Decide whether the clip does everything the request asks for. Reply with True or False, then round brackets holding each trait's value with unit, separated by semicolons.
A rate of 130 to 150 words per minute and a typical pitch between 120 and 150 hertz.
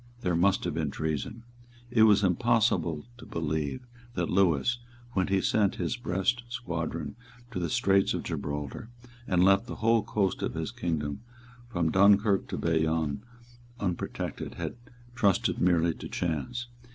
False (145 wpm; 90 Hz)